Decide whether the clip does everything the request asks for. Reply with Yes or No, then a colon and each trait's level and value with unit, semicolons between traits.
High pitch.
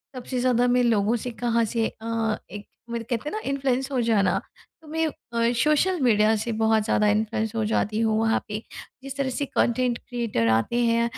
Yes: high, 230 Hz